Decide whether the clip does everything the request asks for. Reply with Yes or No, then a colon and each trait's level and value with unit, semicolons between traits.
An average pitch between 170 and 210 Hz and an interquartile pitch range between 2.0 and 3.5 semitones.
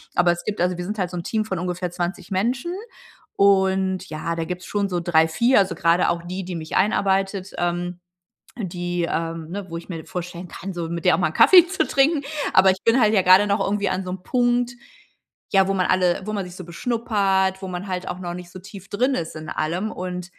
Yes: medium, 185 Hz; narrow, 2.4 semitones